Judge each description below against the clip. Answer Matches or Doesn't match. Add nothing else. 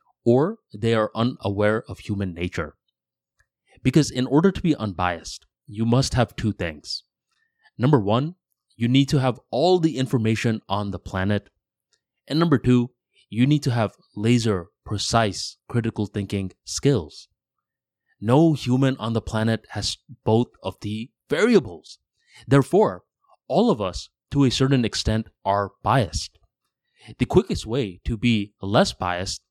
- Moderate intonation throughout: Matches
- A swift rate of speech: Doesn't match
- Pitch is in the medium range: Doesn't match